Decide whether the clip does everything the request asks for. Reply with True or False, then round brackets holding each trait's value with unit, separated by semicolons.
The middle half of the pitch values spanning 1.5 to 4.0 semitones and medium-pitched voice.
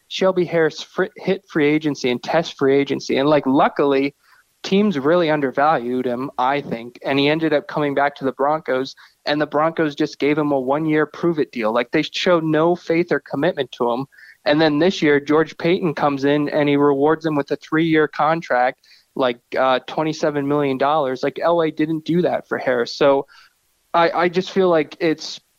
True (2.8 semitones; 150 Hz)